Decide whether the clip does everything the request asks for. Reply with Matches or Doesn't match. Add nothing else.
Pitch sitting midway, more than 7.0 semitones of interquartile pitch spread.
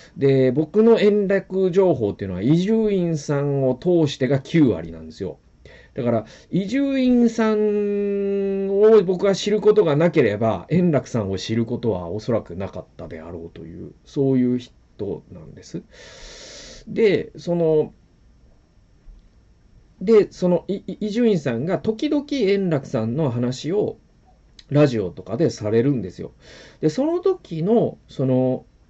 Matches